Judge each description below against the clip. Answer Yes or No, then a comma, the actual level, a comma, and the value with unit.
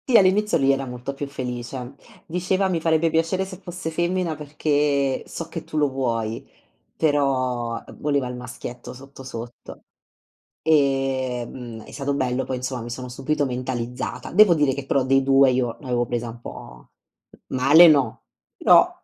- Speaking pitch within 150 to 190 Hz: No, low, 135 Hz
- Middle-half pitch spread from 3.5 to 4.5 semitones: Yes, average, 3.8 semitones